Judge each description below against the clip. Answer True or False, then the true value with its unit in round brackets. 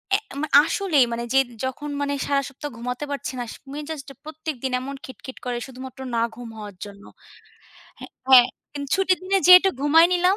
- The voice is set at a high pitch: True (280 Hz)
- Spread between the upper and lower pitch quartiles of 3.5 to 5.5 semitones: True (4.0 semitones)